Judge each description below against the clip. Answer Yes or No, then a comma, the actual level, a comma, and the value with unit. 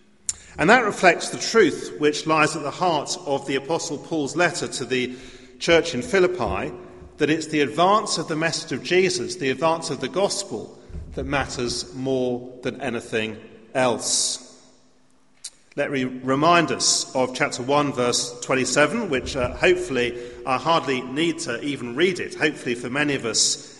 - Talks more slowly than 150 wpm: No, average, 160 wpm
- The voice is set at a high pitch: No, medium, 140 Hz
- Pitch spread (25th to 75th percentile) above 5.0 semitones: No, average, 4.4 semitones